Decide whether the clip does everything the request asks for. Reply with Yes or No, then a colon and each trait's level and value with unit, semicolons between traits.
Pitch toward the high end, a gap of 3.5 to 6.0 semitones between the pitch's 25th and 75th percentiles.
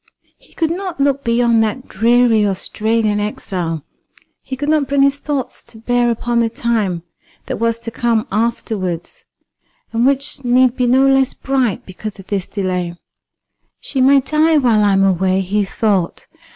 Yes: high, 230 Hz; average, 4.6 semitones